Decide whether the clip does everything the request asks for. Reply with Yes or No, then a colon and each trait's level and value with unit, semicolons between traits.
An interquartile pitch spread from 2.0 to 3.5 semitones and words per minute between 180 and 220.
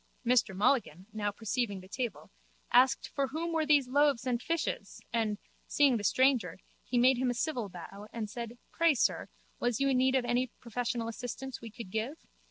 Yes: average, 3.2 semitones; average, 185 wpm